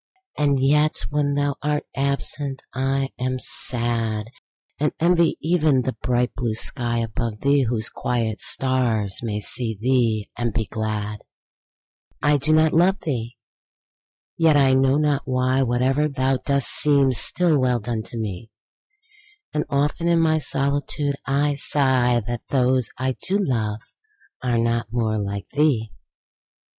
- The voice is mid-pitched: No, low, 130 Hz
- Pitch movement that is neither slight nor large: Yes, average, 3.6 semitones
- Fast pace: No, average, 140 wpm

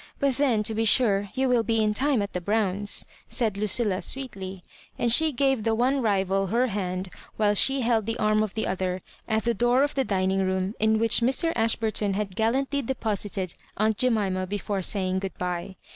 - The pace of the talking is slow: No, fast, 205 wpm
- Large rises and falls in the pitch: No, average, 3.7 semitones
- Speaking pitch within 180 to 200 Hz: No, high, 215 Hz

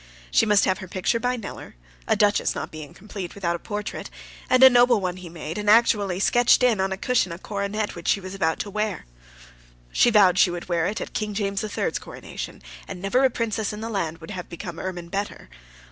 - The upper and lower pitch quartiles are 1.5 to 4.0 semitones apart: Yes, average, 3.1 semitones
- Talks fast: Yes, fast, 225 wpm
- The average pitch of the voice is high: Yes, high, 200 Hz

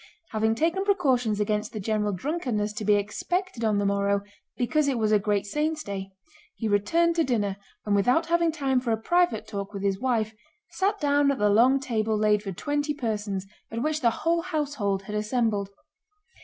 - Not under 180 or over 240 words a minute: Yes, average, 190 wpm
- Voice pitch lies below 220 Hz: No, high, 225 Hz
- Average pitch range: No, wide, 5.9 semitones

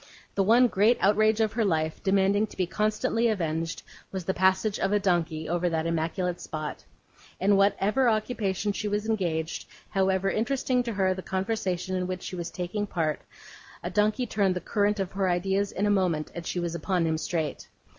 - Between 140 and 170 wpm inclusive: No, average, 190 wpm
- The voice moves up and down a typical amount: Yes, average, 3.1 semitones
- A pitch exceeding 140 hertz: Yes, high, 190 Hz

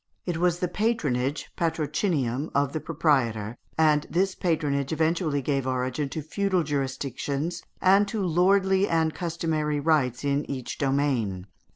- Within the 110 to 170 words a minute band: Yes, slow, 135 wpm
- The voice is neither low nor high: Yes, medium, 150 Hz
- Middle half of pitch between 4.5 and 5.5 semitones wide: No, average, 3.9 semitones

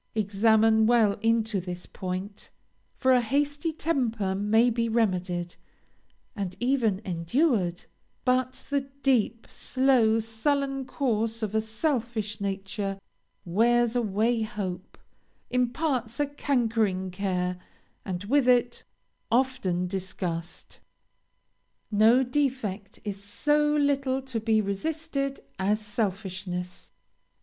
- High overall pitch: Yes, high, 220 Hz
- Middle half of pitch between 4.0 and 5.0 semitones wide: Yes, average, 4.6 semitones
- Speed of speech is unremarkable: No, slow, 105 wpm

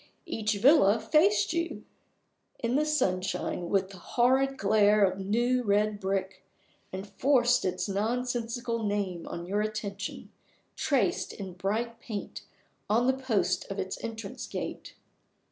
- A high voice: Yes, high, 215 Hz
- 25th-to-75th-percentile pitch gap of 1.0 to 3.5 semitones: No, average, 3.9 semitones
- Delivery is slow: Yes, slow, 130 wpm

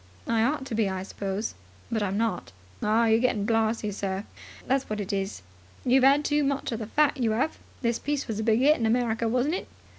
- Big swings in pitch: No, average, 3.8 semitones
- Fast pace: Yes, fast, 220 wpm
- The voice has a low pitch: No, high, 230 Hz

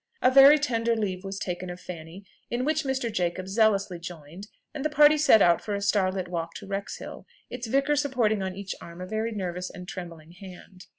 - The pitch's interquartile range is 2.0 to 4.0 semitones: No, average, 4.9 semitones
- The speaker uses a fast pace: Yes, fast, 210 wpm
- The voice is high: Yes, high, 195 Hz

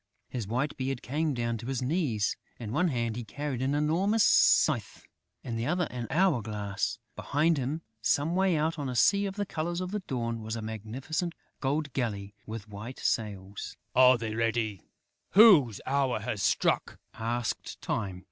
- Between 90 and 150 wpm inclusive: No, average, 170 wpm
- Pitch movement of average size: No, wide, 5.8 semitones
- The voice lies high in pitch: No, low, 125 Hz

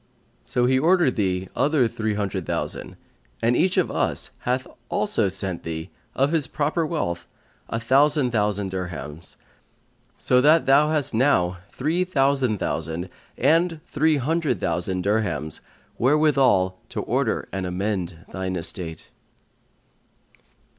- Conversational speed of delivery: No, slow, 125 wpm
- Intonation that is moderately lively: No, wide, 8.1 semitones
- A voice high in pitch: No, low, 115 Hz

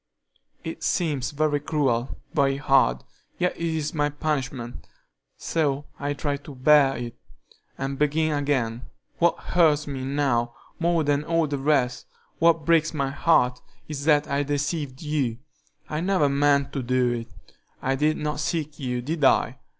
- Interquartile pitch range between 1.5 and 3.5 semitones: Yes, narrow, 2.4 semitones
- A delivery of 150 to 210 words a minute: Yes, average, 155 wpm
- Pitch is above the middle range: No, medium, 145 Hz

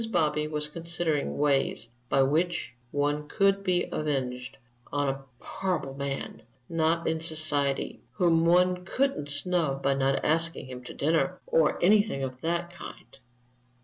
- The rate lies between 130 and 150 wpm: Yes, average, 140 wpm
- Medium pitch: Yes, medium, 155 Hz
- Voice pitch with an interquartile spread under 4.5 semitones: Yes, average, 3.9 semitones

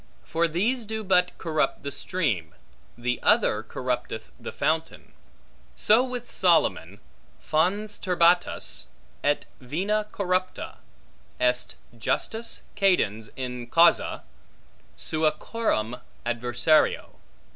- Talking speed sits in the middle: No, slow, 95 wpm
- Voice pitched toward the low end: No, medium, 165 Hz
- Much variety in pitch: Yes, wide, 8.2 semitones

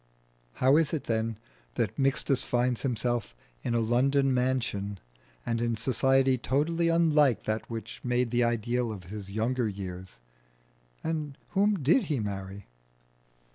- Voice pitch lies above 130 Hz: No, low, 120 Hz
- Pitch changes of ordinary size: Yes, average, 3.8 semitones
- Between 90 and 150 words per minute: Yes, slow, 135 wpm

